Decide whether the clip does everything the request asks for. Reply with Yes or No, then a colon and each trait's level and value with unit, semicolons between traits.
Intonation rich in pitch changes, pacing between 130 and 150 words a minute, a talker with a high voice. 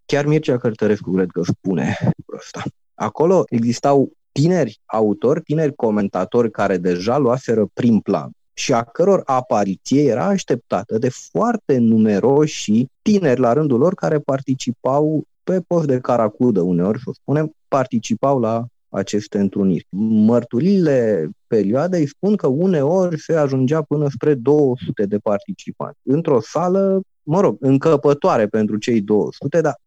No: wide, 5.8 semitones; average, 135 wpm; low, 135 Hz